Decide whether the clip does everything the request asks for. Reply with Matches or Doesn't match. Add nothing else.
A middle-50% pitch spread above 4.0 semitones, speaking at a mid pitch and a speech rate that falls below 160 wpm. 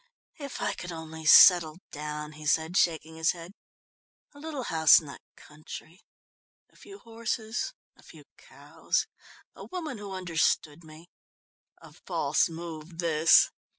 Matches